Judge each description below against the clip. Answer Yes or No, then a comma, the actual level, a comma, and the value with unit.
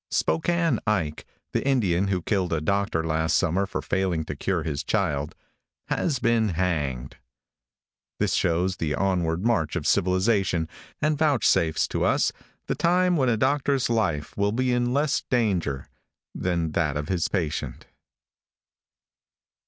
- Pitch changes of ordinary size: No, wide, 6.5 semitones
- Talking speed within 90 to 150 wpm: Yes, average, 140 wpm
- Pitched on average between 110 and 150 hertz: No, very low, 95 Hz